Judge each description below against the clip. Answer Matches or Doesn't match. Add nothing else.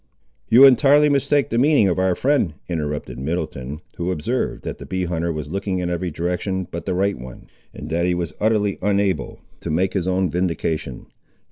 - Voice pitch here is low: Matches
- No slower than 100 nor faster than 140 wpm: Doesn't match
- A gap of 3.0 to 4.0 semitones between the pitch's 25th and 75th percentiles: Matches